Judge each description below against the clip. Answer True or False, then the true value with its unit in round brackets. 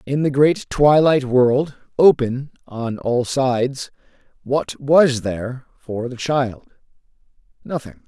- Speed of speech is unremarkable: False (120 wpm)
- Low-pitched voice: True (130 Hz)